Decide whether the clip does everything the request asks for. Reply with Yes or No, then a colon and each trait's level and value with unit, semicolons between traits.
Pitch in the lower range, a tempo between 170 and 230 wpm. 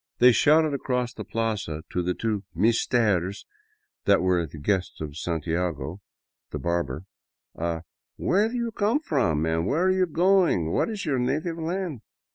Yes: low, 110 Hz; average, 175 wpm